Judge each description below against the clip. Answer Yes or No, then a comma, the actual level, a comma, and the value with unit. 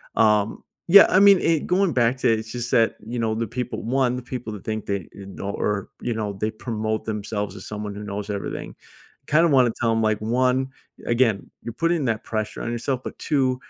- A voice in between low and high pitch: No, low, 115 Hz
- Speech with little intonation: No, average, 3.2 semitones